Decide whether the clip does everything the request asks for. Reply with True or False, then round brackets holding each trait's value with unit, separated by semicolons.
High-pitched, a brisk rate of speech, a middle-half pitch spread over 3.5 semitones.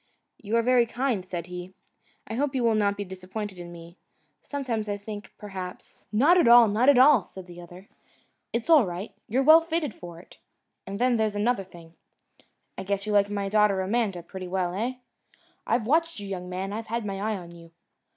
True (205 Hz; 210 wpm; 4.2 semitones)